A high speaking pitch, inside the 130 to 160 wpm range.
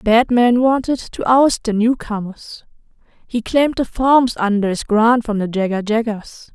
Yes: high, 230 Hz; average, 155 wpm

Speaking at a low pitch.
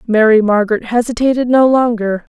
No: high, 230 Hz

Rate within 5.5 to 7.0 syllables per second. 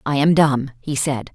No: 4.5 syllables/s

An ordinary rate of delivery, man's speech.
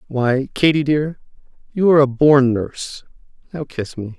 Yes: average, 160 wpm; male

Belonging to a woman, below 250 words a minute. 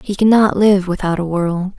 Yes: female; average, 200 wpm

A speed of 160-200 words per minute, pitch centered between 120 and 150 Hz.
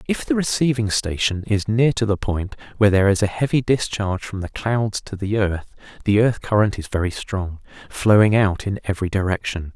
No: average, 190 wpm; low, 105 Hz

